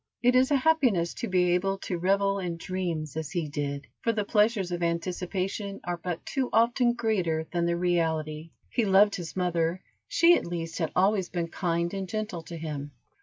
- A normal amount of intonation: Yes, average, 3.3 semitones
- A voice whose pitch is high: No, medium, 180 Hz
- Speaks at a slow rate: No, average, 190 wpm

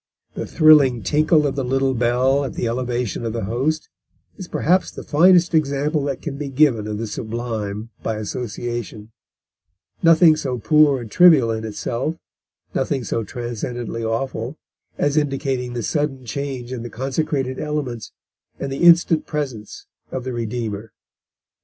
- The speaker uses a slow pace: No, average, 150 wpm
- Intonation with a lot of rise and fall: No, average, 4.2 semitones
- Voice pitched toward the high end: No, low, 130 Hz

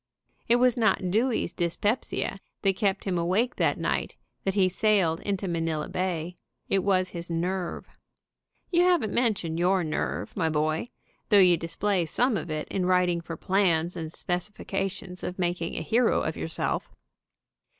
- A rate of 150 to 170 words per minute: Yes, average, 160 wpm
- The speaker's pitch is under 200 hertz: Yes, medium, 185 Hz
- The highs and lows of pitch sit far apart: No, average, 3.2 semitones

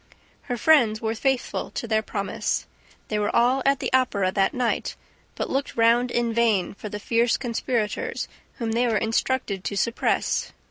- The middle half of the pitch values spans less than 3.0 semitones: Yes, narrow, 2.5 semitones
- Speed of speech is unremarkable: Yes, average, 170 wpm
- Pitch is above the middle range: Yes, high, 230 Hz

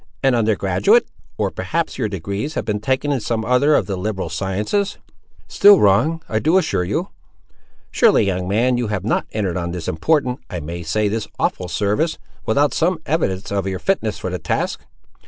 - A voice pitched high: No, low, 105 Hz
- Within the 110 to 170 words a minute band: No, average, 180 wpm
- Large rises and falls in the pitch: Yes, wide, 6.8 semitones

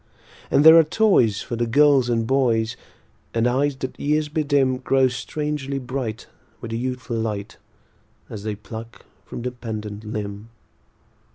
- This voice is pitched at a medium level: No, low, 125 Hz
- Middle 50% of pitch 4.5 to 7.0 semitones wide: No, average, 3.7 semitones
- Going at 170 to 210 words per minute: No, average, 150 wpm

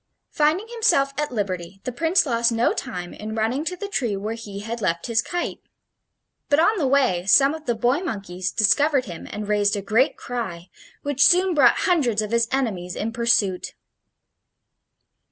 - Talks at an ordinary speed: Yes, average, 175 wpm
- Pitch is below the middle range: No, high, 235 Hz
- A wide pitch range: Yes, wide, 5.9 semitones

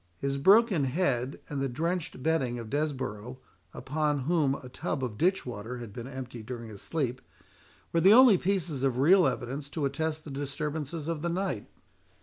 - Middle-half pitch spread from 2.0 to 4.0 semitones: No, average, 4.4 semitones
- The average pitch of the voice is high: No, medium, 140 Hz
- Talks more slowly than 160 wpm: No, average, 175 wpm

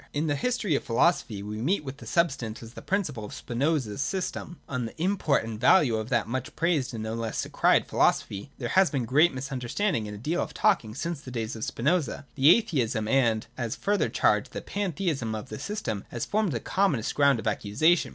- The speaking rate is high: Yes, fast, 210 wpm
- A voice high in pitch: No, low, 135 Hz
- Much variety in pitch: Yes, wide, 7.0 semitones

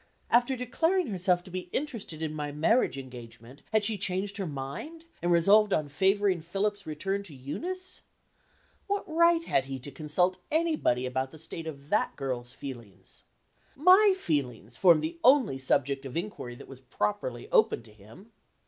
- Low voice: No, medium, 170 Hz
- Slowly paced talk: No, average, 165 wpm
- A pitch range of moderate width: No, wide, 8.0 semitones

